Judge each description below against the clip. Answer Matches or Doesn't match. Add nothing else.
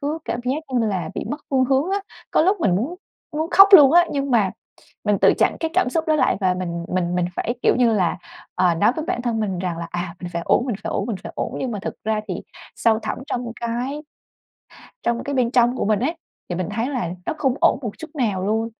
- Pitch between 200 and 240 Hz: Matches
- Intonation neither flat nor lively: Doesn't match